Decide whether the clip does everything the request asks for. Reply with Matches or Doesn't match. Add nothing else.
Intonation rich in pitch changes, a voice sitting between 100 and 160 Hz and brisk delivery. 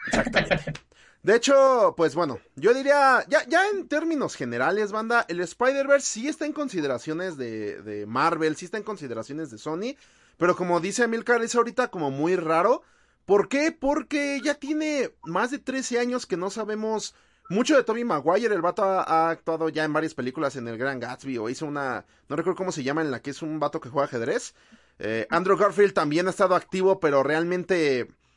Doesn't match